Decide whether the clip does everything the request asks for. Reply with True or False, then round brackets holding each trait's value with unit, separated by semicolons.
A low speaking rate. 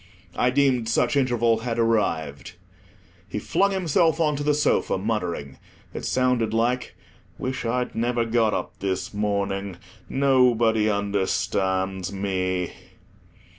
True (115 wpm)